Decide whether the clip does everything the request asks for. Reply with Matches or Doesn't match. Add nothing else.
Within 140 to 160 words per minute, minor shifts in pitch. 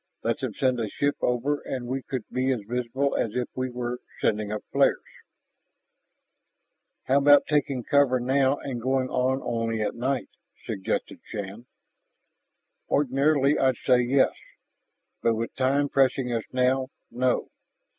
Matches